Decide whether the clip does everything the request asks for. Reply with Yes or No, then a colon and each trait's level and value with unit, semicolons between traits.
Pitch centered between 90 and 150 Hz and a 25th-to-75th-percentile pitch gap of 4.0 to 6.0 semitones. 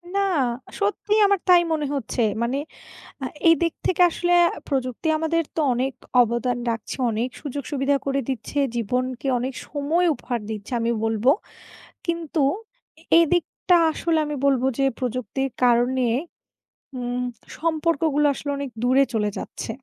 No: very high, 270 Hz; average, 4.6 semitones